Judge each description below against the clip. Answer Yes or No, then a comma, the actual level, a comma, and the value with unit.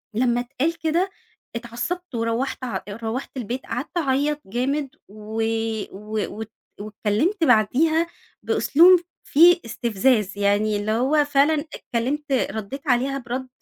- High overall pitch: Yes, very high, 255 Hz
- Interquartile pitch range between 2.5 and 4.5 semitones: No, average, 5.1 semitones